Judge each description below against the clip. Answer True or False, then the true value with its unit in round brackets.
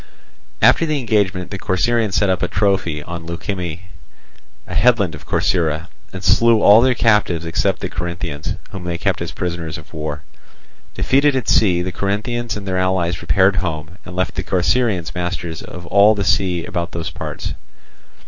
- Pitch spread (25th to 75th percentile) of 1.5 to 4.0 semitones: True (3.3 semitones)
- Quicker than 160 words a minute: True (170 wpm)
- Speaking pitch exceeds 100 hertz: False (95 Hz)